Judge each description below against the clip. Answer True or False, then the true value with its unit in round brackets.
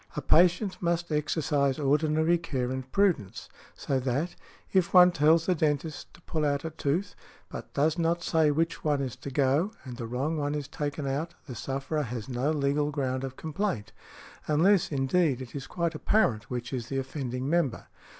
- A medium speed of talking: True (180 wpm)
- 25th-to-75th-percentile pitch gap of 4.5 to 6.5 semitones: False (3.7 semitones)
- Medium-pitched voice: True (150 Hz)